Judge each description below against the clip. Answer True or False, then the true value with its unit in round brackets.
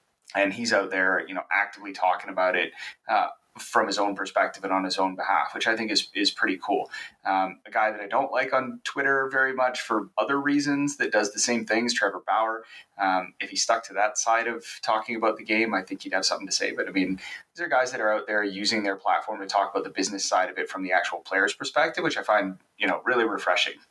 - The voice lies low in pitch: True (110 Hz)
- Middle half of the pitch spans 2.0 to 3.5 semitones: False (4.0 semitones)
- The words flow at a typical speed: False (250 wpm)